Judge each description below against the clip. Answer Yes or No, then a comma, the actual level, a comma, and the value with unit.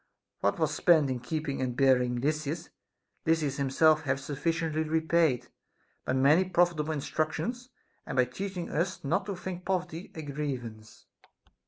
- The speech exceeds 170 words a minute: No, average, 140 wpm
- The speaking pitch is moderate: Yes, medium, 155 Hz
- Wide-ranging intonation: No, average, 3.8 semitones